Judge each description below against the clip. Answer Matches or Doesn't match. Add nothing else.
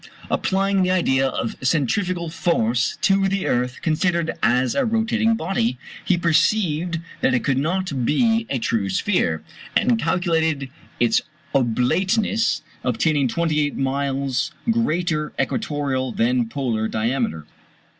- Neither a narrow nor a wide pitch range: Doesn't match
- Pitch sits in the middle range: Matches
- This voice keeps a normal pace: Doesn't match